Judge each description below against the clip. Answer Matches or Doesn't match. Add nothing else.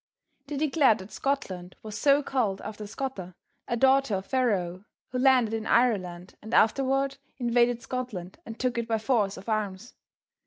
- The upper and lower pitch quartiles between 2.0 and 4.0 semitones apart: Doesn't match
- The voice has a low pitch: Doesn't match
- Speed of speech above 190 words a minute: Doesn't match